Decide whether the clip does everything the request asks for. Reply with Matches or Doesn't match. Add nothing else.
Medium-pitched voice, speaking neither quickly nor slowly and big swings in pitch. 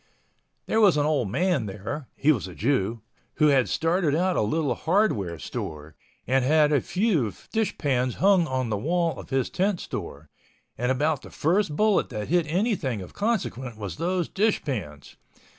Matches